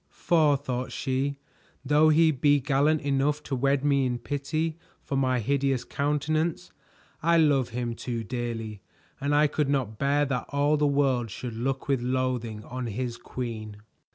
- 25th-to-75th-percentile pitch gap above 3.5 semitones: No, average, 2.9 semitones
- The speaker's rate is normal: Yes, average, 160 wpm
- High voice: No, low, 135 Hz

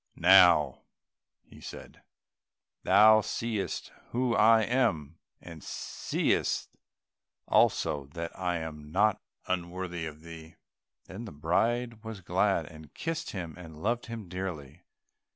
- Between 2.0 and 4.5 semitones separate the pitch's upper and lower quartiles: No, wide, 5.4 semitones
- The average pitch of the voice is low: Yes, very low, 90 Hz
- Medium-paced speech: No, slow, 115 wpm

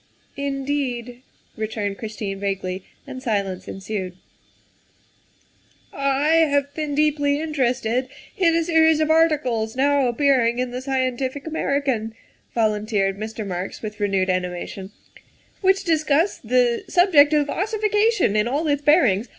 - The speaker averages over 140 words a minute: No, slow, 135 wpm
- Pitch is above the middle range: Yes, very high, 260 Hz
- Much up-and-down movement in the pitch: Yes, wide, 5.7 semitones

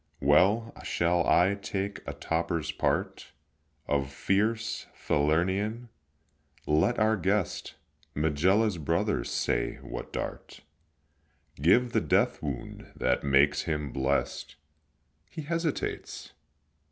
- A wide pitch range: Yes, wide, 6.3 semitones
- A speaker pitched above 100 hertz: No, very low, 85 Hz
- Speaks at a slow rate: Yes, slow, 100 wpm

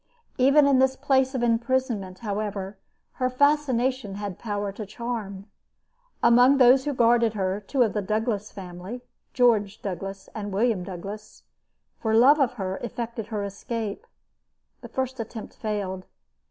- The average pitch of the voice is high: Yes, high, 225 Hz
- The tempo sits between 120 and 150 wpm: Yes, average, 140 wpm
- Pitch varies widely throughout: No, average, 3.9 semitones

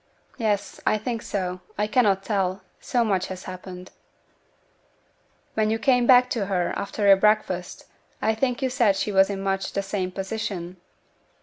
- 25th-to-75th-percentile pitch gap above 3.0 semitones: No, average, 2.7 semitones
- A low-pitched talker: No, high, 200 Hz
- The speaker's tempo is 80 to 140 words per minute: No, average, 165 wpm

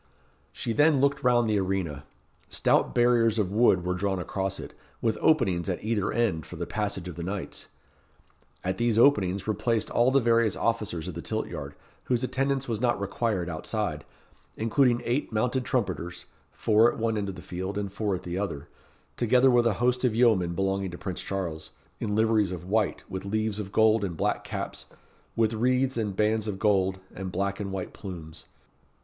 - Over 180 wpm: Yes, average, 190 wpm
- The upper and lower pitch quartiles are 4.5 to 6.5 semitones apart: No, average, 3.8 semitones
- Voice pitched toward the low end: Yes, low, 105 Hz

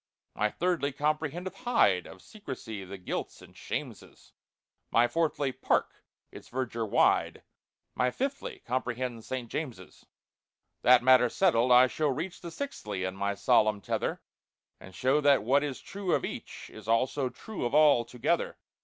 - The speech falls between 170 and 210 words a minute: No, average, 145 wpm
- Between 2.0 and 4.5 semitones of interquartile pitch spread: No, average, 5.2 semitones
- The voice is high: No, low, 130 Hz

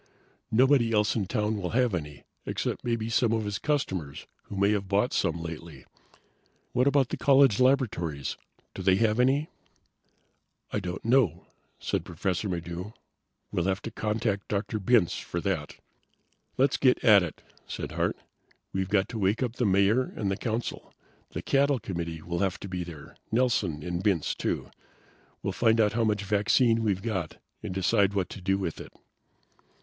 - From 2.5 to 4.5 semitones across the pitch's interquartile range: Yes, average, 4.1 semitones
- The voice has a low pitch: Yes, low, 105 Hz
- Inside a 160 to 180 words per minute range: Yes, average, 170 wpm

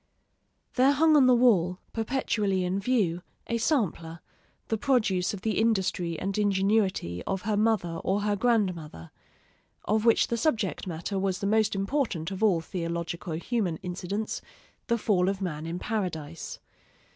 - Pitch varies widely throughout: No, average, 4.1 semitones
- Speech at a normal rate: Yes, average, 150 wpm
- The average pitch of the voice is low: No, high, 195 Hz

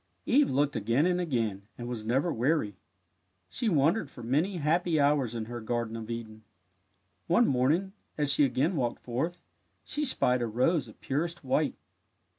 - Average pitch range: No, wide, 5.8 semitones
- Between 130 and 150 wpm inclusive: No, average, 165 wpm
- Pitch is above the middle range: No, low, 135 Hz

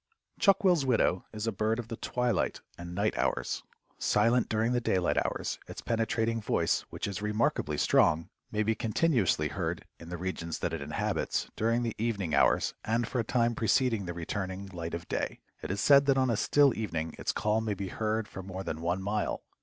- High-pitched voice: No, low, 110 Hz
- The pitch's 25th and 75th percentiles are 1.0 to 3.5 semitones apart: No, average, 3.9 semitones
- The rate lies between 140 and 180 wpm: No, average, 200 wpm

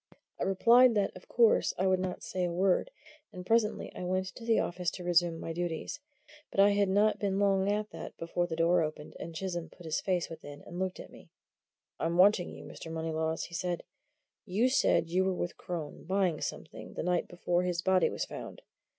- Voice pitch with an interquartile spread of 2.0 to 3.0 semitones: Yes, narrow, 2.4 semitones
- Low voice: No, medium, 180 Hz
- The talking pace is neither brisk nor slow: No, fast, 210 wpm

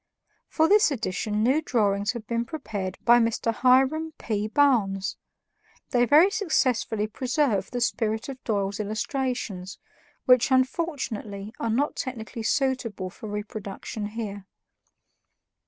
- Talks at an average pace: No, slow, 120 wpm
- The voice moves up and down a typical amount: Yes, average, 4.1 semitones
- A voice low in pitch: No, high, 230 Hz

